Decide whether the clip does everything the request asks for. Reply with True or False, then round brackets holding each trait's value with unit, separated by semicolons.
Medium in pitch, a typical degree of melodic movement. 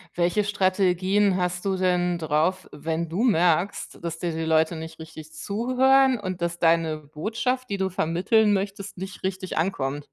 True (180 Hz; 3.5 semitones)